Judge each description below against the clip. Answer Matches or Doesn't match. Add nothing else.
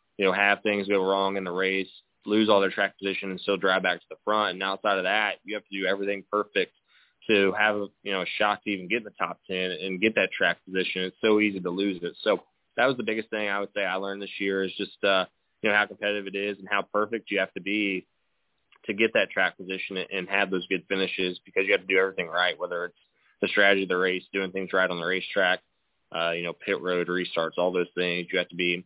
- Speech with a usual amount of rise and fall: Doesn't match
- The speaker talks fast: Matches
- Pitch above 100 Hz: Doesn't match